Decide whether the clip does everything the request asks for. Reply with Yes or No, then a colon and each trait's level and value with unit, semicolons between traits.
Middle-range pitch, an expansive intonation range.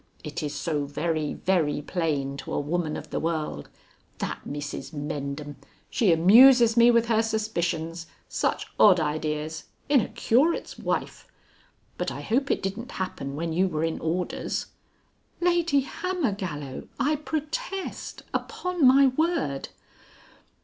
Yes: medium, 175 Hz; wide, 8.9 semitones